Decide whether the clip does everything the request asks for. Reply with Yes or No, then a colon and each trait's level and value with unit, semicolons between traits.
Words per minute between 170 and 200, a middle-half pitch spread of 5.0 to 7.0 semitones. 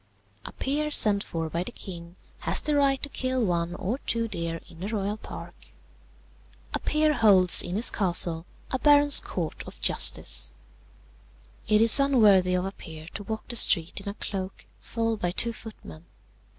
Yes: average, 175 wpm; average, 5.3 semitones